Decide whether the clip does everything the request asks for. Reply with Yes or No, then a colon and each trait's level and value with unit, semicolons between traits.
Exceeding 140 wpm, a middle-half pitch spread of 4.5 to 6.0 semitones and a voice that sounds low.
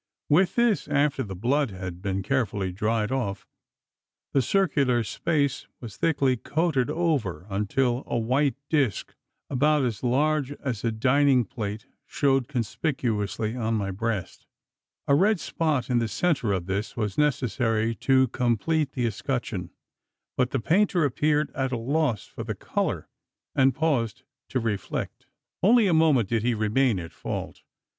Yes: average, 150 wpm; average, 4.8 semitones; low, 125 Hz